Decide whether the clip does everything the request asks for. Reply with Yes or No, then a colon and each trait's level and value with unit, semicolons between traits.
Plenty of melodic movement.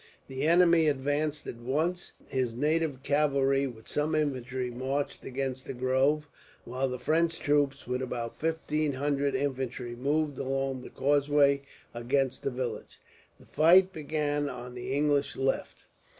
No: narrow, 2.5 semitones